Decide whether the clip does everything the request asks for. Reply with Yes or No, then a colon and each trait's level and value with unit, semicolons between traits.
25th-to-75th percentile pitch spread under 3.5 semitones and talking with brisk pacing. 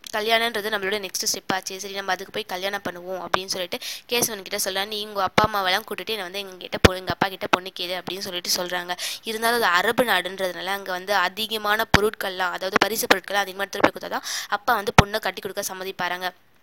Yes: narrow, 2.4 semitones; fast, 190 wpm